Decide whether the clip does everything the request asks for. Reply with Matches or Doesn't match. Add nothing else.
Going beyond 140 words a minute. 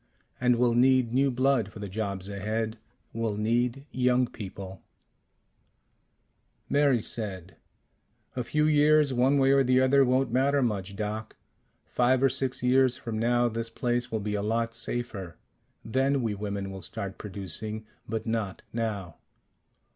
Matches